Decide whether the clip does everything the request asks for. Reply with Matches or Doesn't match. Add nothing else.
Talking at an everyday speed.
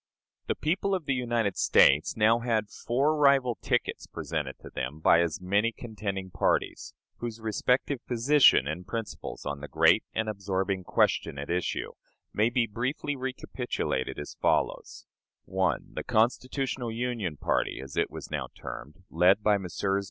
Matches